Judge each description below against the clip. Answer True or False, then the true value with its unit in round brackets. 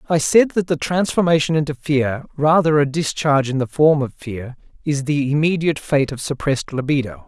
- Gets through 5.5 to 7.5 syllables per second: False (5.3 syllables/s)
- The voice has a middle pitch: True (145 Hz)